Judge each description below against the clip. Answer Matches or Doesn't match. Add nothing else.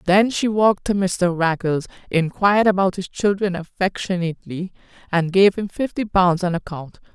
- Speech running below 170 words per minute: Matches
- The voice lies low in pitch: Doesn't match